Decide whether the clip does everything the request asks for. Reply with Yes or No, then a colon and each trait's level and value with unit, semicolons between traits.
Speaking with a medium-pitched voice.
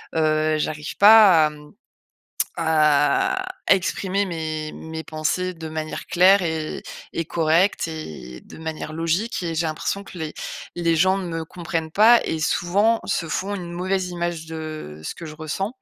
Yes: medium, 165 Hz